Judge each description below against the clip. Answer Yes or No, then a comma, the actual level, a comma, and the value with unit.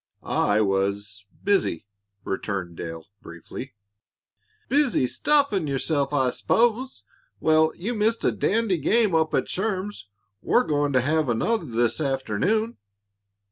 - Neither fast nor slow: No, slow, 120 wpm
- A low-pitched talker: No, medium, 155 Hz